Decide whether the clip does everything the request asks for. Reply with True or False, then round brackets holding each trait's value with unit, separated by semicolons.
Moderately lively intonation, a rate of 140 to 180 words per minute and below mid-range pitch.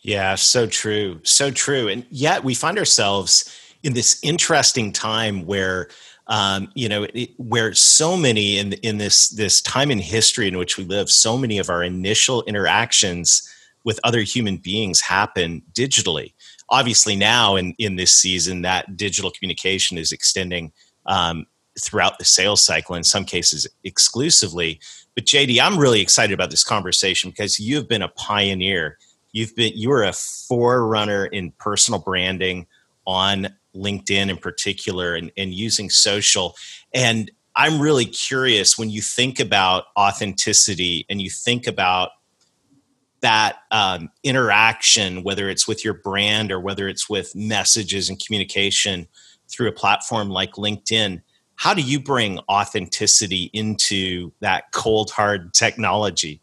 True (3.1 semitones; 145 wpm; 100 Hz)